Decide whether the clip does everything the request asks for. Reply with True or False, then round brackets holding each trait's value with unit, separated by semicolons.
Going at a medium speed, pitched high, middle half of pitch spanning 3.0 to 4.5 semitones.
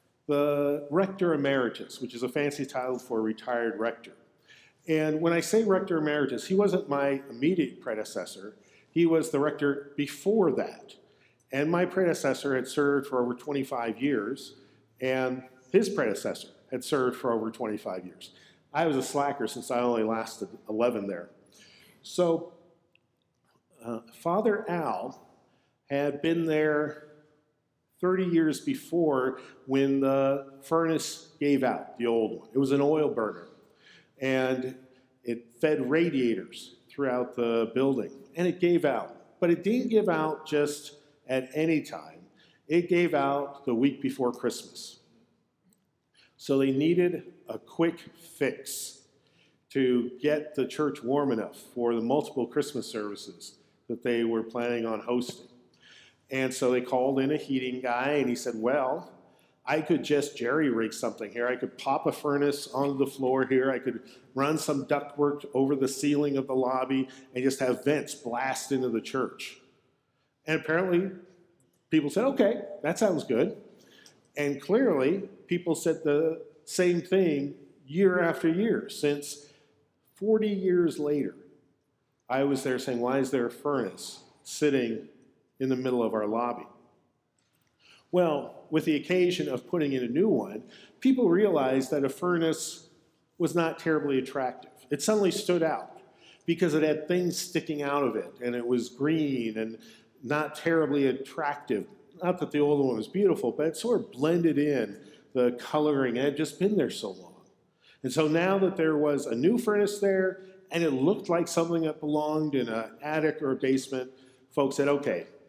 False (155 wpm; 145 Hz; 3.9 semitones)